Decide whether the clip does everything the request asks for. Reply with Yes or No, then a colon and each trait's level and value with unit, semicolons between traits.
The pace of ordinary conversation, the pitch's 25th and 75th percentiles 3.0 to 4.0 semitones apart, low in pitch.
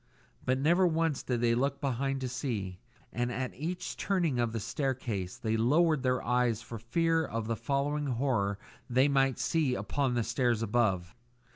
Yes: average, 170 wpm; average, 3.5 semitones; low, 125 Hz